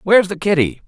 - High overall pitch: No, medium, 180 Hz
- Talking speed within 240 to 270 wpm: No, fast, 205 wpm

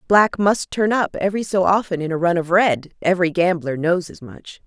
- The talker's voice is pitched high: No, medium, 180 Hz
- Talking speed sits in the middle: No, fast, 220 wpm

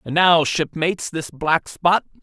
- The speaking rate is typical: Yes, average, 160 wpm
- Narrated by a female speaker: No, male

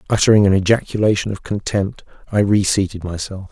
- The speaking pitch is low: Yes, low, 100 Hz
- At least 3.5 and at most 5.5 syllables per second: No, 5.9 syllables/s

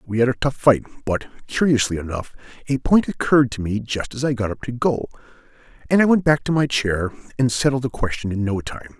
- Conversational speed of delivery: No, fast, 225 wpm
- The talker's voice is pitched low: Yes, low, 125 Hz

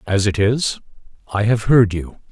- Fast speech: No, average, 180 wpm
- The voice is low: Yes, low, 105 Hz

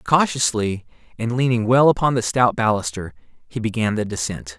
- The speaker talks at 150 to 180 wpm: Yes, average, 155 wpm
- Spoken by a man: Yes, male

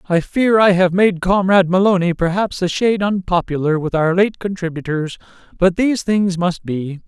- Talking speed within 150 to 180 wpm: Yes, average, 170 wpm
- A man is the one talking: Yes, male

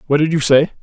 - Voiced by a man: Yes, male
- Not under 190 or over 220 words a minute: No, fast, 290 wpm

